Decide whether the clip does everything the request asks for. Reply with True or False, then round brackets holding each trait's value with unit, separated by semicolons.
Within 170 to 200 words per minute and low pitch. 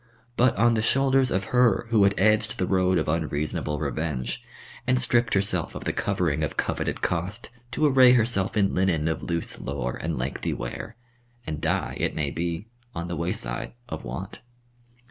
True (175 wpm; 95 Hz)